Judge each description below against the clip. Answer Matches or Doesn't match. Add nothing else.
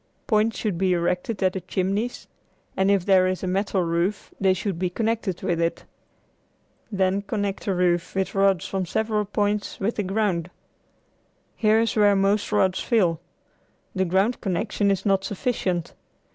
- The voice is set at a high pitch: Matches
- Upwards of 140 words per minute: Matches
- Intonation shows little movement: Matches